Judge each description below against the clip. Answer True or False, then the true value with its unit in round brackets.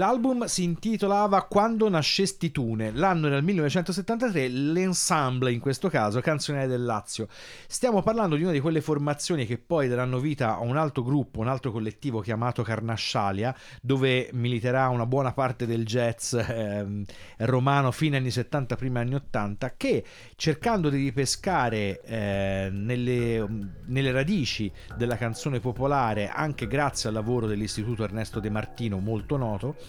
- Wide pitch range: False (5.0 semitones)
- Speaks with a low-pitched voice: True (130 Hz)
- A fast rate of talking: False (145 wpm)